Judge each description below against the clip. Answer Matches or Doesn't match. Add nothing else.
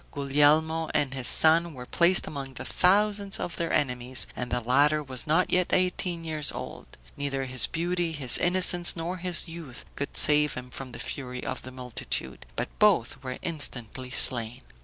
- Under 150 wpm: Doesn't match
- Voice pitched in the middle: Matches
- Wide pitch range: Doesn't match